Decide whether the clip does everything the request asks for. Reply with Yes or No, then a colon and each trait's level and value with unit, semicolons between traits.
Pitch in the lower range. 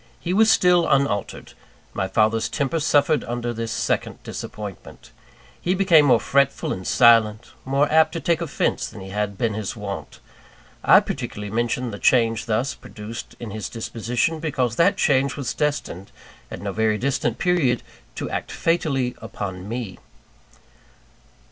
Yes: low, 120 Hz